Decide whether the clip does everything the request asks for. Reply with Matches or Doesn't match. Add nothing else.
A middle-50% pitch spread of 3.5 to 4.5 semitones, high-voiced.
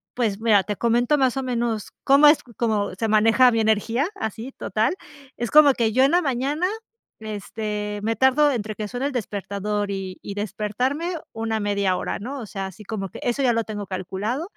Matches